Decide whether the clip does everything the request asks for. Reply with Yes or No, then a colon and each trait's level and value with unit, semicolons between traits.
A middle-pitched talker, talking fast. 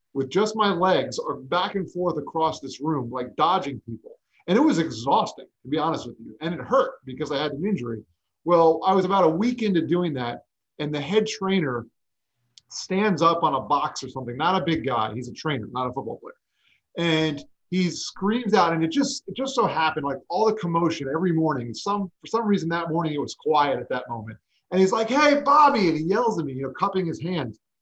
Yes: medium, 165 Hz; fast, 230 wpm